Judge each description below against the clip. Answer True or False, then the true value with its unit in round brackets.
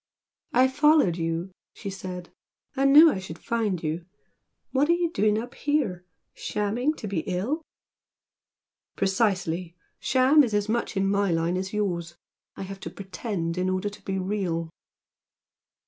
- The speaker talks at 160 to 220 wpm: False (150 wpm)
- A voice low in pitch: False (195 Hz)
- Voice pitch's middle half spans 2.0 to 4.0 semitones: False (4.9 semitones)